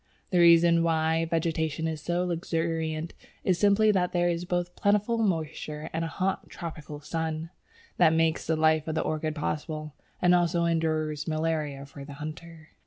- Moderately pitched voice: Yes, medium, 165 Hz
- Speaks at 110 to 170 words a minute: Yes, average, 165 wpm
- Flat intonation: Yes, narrow, 1.8 semitones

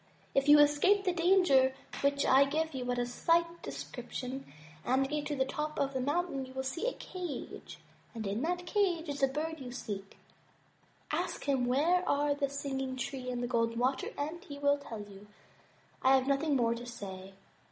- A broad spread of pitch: No, average, 3.7 semitones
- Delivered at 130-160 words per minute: No, average, 195 wpm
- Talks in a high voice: Yes, very high, 275 Hz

